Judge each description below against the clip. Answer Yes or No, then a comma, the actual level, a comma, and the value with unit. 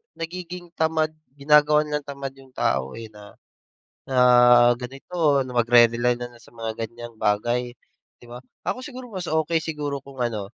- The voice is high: No, low, 135 Hz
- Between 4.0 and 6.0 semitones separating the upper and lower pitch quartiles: Yes, average, 4.6 semitones